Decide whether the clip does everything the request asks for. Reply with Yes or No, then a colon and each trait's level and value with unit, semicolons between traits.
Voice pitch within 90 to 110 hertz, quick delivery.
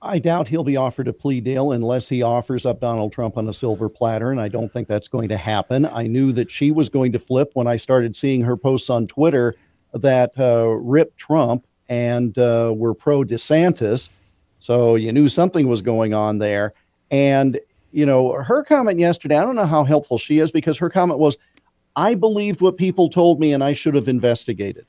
No: low, 130 Hz; fast, 210 wpm